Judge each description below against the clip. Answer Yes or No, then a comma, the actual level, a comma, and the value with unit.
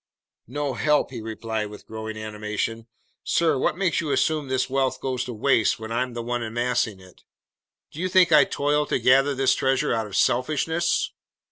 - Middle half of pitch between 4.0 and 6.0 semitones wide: Yes, average, 4.5 semitones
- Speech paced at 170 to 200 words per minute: Yes, average, 180 wpm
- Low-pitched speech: Yes, low, 130 Hz